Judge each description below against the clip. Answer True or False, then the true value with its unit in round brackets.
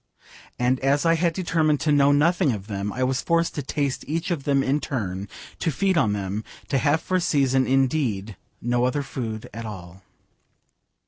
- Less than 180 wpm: False (190 wpm)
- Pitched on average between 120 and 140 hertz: True (135 Hz)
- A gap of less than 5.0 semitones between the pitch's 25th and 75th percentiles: False (5.5 semitones)